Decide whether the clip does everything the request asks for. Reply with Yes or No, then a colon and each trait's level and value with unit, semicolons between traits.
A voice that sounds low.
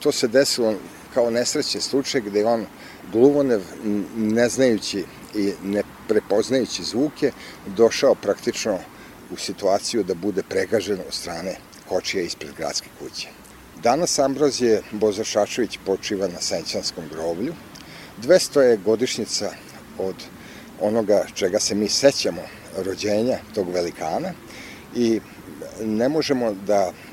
Yes: low, 110 Hz